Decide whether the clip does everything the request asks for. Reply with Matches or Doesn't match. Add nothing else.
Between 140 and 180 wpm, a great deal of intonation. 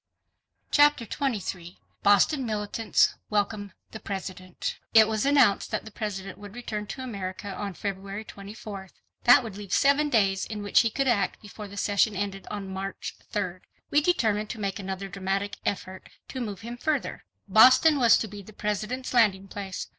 Doesn't match